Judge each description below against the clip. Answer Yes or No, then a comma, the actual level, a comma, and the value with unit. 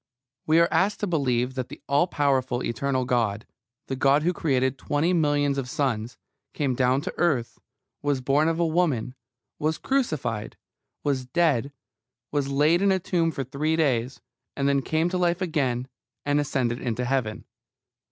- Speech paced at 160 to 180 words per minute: Yes, average, 165 wpm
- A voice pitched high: No, medium, 140 Hz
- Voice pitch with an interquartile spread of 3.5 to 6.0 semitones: Yes, average, 4.0 semitones